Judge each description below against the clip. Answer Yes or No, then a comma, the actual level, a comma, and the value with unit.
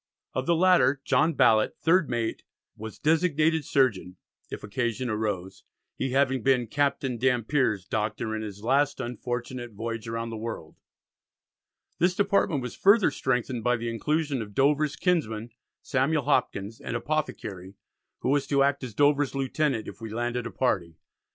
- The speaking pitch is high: No, low, 125 Hz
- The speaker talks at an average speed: Yes, average, 150 wpm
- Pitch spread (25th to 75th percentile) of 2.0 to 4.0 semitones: No, average, 4.4 semitones